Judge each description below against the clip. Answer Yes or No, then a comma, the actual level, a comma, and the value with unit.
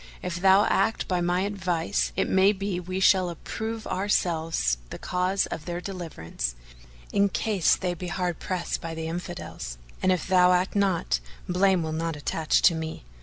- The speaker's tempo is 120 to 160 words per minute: No, average, 170 wpm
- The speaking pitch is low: No, medium, 180 Hz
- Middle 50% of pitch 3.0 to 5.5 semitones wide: No, narrow, 2.6 semitones